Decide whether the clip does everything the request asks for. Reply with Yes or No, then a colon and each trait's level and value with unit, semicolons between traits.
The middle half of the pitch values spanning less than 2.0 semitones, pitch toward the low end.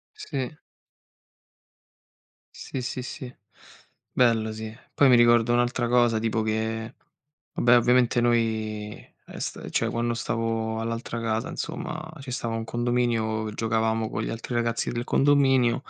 Yes: narrow, 1.5 semitones; low, 115 Hz